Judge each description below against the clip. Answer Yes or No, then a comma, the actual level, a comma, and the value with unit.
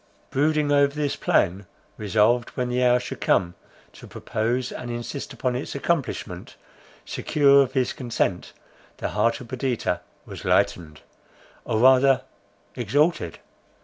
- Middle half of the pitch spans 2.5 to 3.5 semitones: No, average, 4.0 semitones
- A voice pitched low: Yes, low, 125 Hz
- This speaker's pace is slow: Yes, slow, 130 wpm